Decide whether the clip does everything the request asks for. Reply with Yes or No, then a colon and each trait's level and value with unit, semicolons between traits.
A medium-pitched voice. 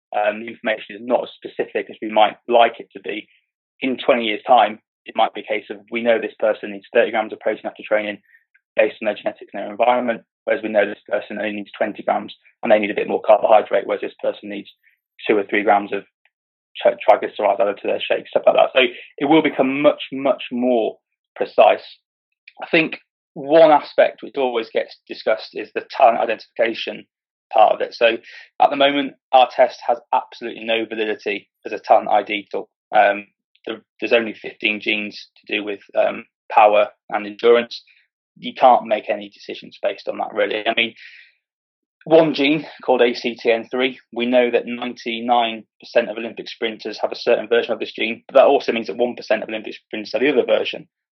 No: low, 120 Hz